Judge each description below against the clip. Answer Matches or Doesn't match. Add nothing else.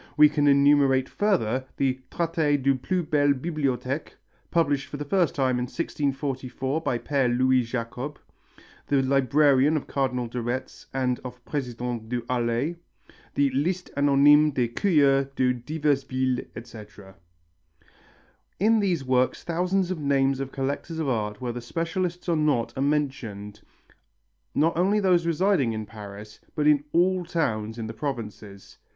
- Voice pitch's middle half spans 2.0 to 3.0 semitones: Doesn't match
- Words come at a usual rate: Matches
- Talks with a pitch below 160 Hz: Matches